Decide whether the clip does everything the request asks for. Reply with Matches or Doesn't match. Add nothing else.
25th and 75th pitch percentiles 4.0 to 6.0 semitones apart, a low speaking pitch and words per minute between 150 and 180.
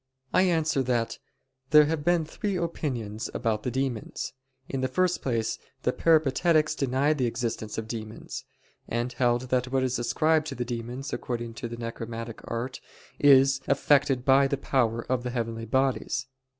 Doesn't match